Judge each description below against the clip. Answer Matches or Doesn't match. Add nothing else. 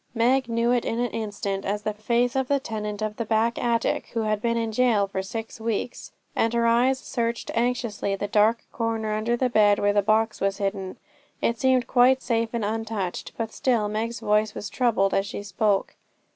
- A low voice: Doesn't match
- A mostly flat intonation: Matches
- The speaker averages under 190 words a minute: Doesn't match